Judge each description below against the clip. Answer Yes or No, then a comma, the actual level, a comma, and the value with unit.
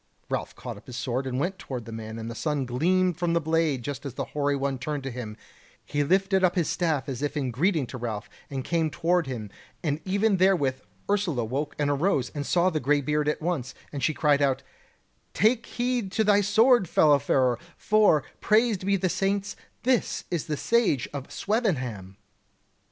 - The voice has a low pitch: No, medium, 150 Hz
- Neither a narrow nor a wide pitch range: No, wide, 6.1 semitones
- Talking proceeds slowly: No, average, 195 wpm